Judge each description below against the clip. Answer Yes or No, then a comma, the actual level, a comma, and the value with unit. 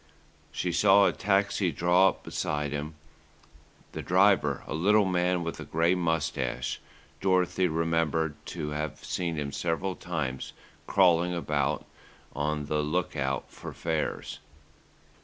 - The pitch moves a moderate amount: Yes, average, 3.2 semitones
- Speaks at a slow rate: Yes, slow, 130 wpm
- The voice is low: Yes, very low, 80 Hz